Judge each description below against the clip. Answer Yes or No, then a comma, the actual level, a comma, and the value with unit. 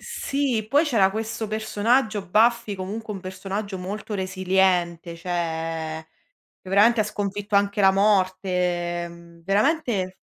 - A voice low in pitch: No, high, 195 Hz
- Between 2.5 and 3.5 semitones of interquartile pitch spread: Yes, average, 2.8 semitones